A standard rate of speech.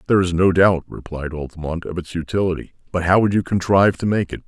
No: fast, 230 wpm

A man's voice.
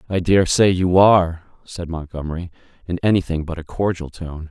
Yes: male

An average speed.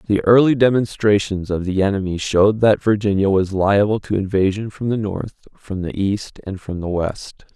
Yes: average, 185 wpm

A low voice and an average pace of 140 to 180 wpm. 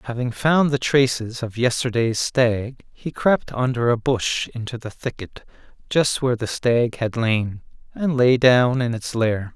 Yes: low, 120 Hz; average, 170 wpm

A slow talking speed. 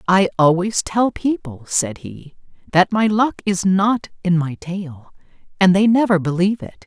No: average, 165 wpm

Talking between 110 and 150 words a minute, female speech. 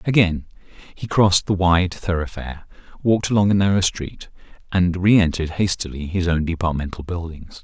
No: average, 140 wpm; male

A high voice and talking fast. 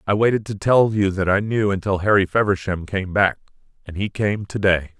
No: low, 100 Hz; fast, 215 wpm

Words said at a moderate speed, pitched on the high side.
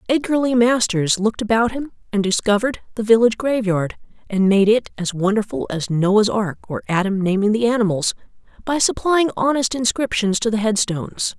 Yes: average, 165 wpm; high, 220 Hz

